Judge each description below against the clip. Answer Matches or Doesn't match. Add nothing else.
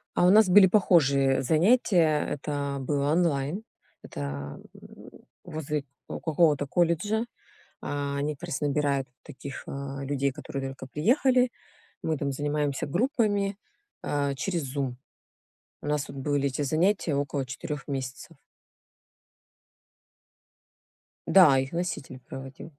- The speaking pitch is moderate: Matches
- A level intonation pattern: Doesn't match